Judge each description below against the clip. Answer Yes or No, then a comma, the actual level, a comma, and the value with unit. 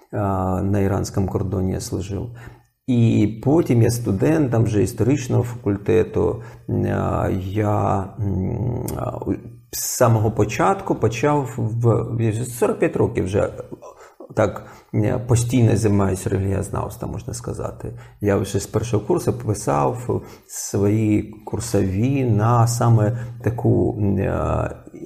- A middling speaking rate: No, slow, 95 wpm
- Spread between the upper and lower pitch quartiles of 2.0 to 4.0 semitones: Yes, average, 3.2 semitones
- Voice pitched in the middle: No, low, 110 Hz